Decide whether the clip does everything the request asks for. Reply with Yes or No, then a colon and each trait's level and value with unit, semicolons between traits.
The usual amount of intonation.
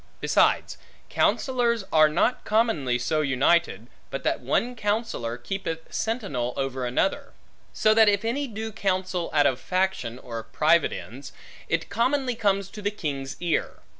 No: wide, 8.3 semitones